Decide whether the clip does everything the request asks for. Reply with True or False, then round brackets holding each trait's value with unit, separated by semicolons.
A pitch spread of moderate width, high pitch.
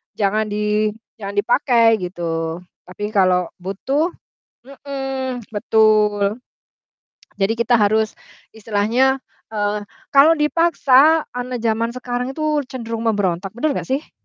True (4.3 semitones; 225 Hz)